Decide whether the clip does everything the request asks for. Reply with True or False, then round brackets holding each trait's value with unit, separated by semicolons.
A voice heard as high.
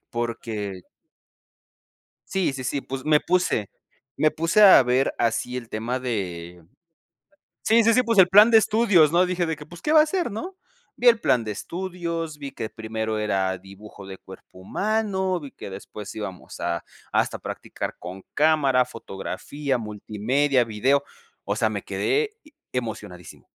False (135 Hz)